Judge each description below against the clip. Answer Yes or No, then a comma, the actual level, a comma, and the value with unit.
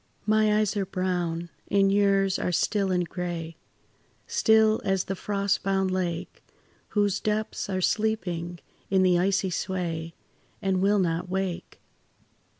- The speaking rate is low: Yes, slow, 130 wpm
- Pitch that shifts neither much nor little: No, narrow, 2.2 semitones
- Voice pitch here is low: No, high, 190 Hz